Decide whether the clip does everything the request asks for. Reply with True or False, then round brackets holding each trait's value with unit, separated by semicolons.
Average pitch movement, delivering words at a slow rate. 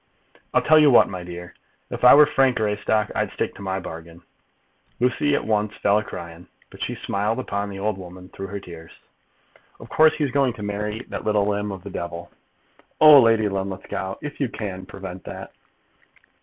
False (3.5 semitones; 190 wpm)